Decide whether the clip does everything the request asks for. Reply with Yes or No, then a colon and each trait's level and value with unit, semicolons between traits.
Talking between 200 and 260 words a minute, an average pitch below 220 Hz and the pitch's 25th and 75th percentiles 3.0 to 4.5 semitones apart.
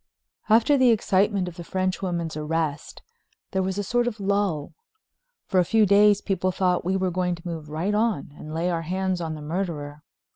Yes: fast, 205 wpm; medium, 185 Hz; average, 3.4 semitones